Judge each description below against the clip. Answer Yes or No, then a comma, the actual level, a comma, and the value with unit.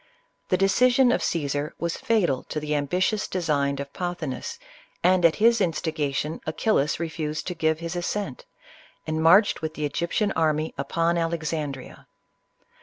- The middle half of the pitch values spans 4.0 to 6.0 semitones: No, average, 3.3 semitones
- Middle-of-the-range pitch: Yes, medium, 165 Hz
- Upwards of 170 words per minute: No, average, 145 wpm